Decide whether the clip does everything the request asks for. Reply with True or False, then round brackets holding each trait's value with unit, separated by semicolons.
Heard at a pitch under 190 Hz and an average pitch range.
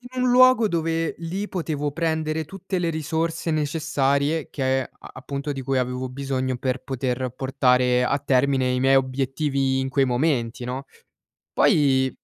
True (140 Hz; 3.4 semitones)